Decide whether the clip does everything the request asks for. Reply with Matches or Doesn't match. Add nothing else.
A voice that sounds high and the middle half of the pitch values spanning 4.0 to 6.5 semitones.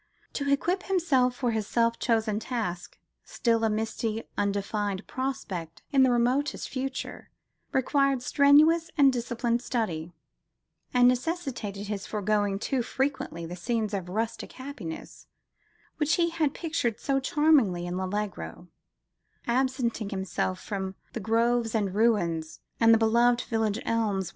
Matches